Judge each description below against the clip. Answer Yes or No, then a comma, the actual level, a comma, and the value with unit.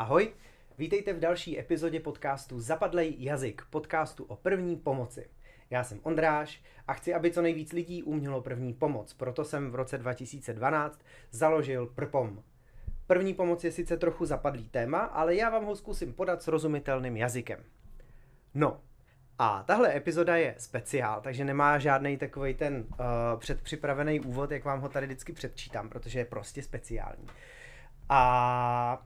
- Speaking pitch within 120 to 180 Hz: Yes, medium, 140 Hz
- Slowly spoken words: No, average, 150 wpm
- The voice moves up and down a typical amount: Yes, average, 4.0 semitones